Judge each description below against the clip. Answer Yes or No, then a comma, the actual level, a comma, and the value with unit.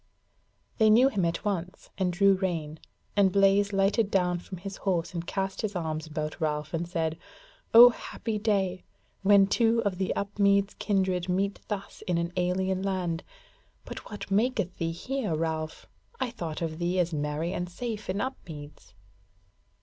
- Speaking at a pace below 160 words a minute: No, average, 165 wpm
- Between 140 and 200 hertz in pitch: Yes, medium, 185 Hz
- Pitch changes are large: No, average, 3.0 semitones